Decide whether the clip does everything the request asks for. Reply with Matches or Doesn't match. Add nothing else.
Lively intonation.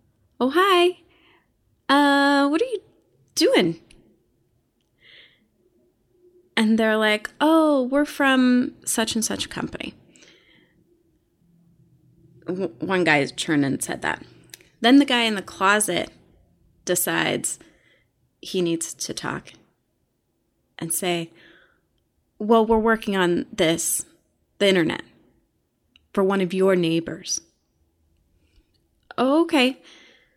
Matches